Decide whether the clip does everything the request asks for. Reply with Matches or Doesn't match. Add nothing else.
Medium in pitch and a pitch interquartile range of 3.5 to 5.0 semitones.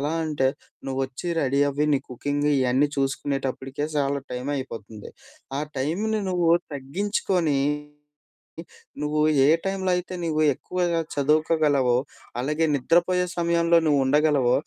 Matches